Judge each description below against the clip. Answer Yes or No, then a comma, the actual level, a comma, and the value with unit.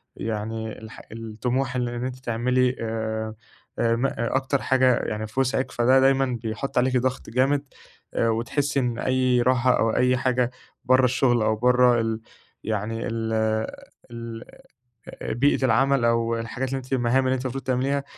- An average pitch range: No, narrow, 2.3 semitones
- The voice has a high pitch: No, low, 125 Hz